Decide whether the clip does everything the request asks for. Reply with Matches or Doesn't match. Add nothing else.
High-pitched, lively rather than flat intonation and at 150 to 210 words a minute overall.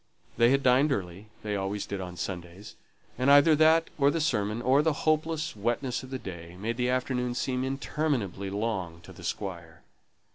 Doesn't match